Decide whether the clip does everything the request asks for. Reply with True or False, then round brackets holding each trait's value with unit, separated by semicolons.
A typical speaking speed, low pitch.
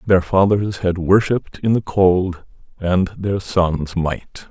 True (145 wpm; 95 Hz)